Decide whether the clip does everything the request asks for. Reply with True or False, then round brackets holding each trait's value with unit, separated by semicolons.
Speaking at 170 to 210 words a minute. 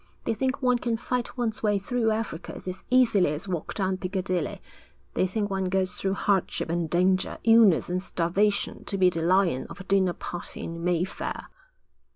True (180 wpm)